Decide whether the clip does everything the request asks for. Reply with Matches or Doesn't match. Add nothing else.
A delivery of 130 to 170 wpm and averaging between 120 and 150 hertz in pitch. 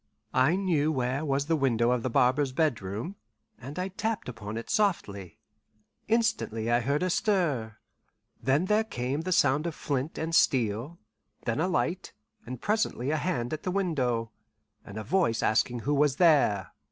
Matches